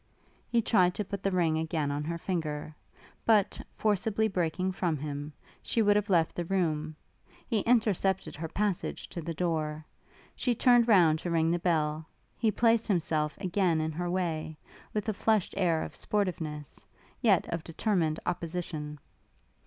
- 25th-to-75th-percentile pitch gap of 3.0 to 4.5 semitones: Yes, average, 4.2 semitones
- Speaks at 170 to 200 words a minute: No, average, 160 wpm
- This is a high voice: No, medium, 175 Hz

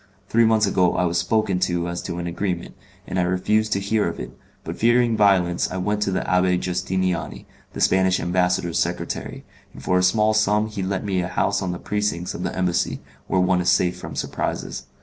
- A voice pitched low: Yes, very low, 95 Hz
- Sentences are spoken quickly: Yes, fast, 210 wpm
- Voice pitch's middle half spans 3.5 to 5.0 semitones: No, average, 2.7 semitones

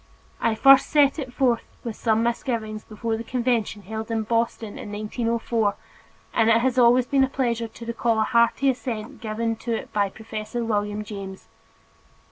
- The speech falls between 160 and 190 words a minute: Yes, average, 165 wpm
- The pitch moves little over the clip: Yes, narrow, 1.9 semitones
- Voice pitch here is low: No, high, 230 Hz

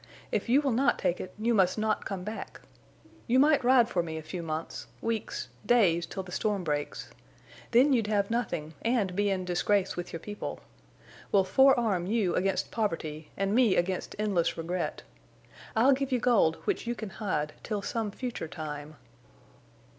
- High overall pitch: Yes, high, 200 Hz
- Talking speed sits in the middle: Yes, average, 165 wpm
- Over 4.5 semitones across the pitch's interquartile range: Yes, average, 5.1 semitones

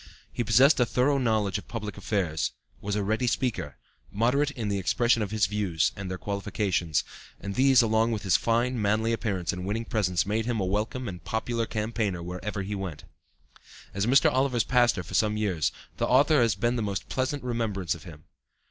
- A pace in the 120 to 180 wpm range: No, average, 190 wpm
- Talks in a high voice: No, low, 105 Hz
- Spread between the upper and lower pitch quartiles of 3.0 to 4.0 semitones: Yes, average, 3.4 semitones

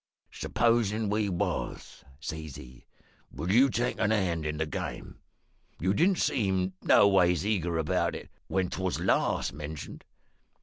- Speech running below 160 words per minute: Yes, slow, 135 wpm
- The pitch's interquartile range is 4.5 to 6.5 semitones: Yes, average, 5.1 semitones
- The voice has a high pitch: No, very low, 95 Hz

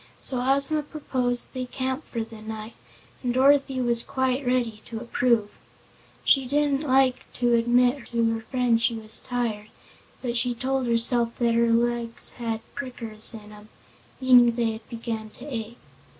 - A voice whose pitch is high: Yes, high, 240 Hz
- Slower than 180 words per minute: Yes, average, 160 wpm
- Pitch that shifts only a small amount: Yes, narrow, 2.2 semitones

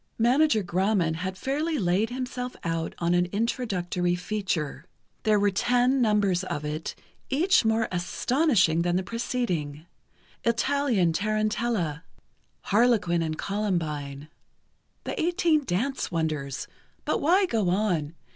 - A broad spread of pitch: Yes, wide, 6.0 semitones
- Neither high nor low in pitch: No, high, 200 Hz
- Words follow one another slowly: Yes, slow, 120 wpm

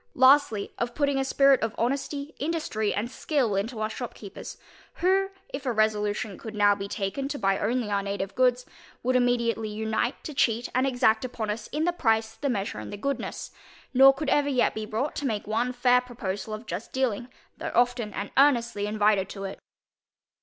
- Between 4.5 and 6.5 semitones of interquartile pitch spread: No, average, 3.9 semitones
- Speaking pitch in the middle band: No, high, 235 Hz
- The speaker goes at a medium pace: Yes, average, 190 wpm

